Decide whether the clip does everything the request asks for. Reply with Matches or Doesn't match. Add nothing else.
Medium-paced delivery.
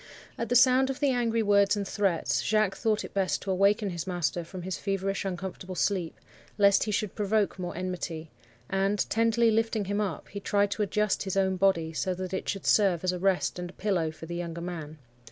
Doesn't match